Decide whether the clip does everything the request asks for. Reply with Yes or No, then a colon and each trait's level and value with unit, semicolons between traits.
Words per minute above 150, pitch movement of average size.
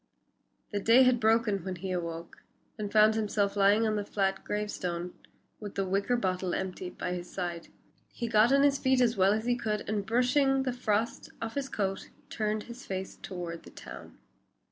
Yes: average, 190 wpm; average, 3.6 semitones